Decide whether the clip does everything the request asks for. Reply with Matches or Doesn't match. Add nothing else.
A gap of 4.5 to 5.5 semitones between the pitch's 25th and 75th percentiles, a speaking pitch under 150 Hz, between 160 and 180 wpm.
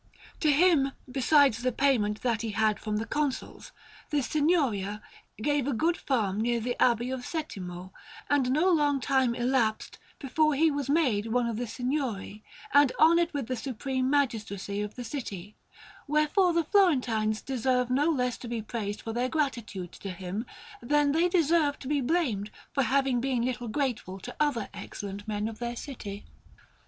Doesn't match